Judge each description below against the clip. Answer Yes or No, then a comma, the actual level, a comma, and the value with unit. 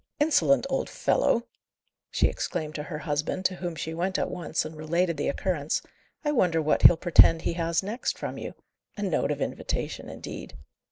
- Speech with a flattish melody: No, average, 3.2 semitones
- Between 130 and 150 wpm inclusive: No, average, 180 wpm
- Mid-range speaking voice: Yes, medium, 170 Hz